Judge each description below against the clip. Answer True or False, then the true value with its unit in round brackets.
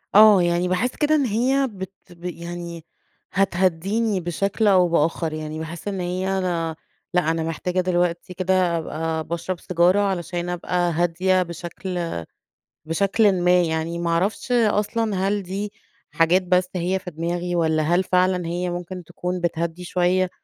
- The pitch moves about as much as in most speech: False (1.9 semitones)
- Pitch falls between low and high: True (180 Hz)